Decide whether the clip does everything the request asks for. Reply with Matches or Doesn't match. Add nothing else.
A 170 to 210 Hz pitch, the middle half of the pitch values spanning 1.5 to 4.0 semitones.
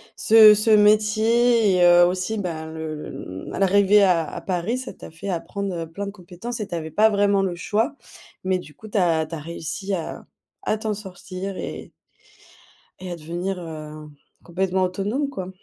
Matches